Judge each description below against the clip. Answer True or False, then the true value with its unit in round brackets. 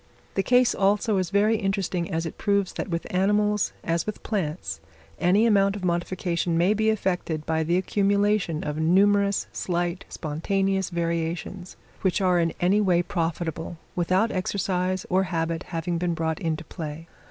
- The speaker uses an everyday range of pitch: True (3.0 semitones)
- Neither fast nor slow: True (155 wpm)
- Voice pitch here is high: False (180 Hz)